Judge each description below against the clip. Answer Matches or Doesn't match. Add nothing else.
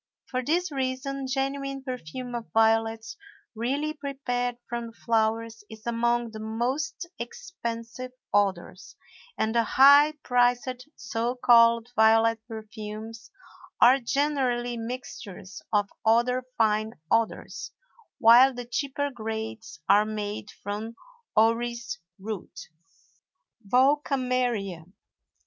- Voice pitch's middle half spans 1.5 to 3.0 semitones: Matches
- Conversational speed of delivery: Doesn't match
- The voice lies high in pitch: Matches